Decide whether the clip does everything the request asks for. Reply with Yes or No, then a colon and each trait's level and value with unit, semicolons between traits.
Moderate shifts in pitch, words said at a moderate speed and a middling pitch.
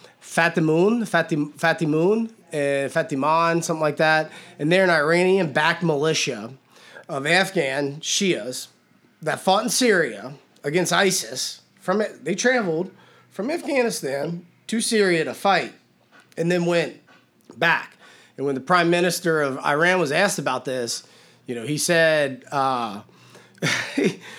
No: average, 4.1 semitones; slow, 125 wpm; medium, 165 Hz